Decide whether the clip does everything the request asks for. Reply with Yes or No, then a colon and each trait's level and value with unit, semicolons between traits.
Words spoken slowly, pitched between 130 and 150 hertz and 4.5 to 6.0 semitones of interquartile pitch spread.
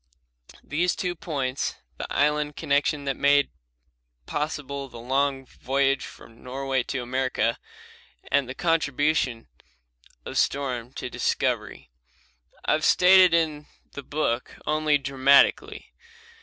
No: slow, 115 wpm; medium, 140 Hz; narrow, 2.4 semitones